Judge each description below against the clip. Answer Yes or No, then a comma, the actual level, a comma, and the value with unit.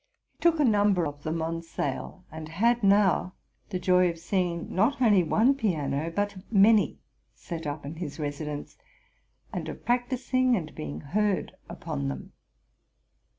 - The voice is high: No, medium, 180 Hz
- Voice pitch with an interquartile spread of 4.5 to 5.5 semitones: Yes, average, 5.2 semitones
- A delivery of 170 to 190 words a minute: No, average, 155 wpm